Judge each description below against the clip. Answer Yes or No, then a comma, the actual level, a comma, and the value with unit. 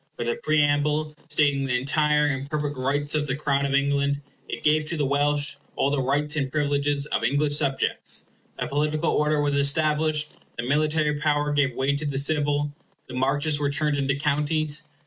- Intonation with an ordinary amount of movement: No, narrow, 1.2 semitones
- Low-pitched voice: No, medium, 145 Hz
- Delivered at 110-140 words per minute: No, average, 185 wpm